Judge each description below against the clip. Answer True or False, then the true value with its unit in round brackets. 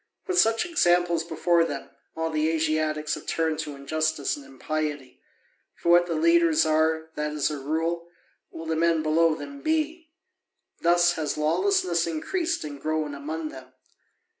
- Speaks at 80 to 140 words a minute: False (155 wpm)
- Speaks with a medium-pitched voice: True (160 Hz)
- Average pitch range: False (1.9 semitones)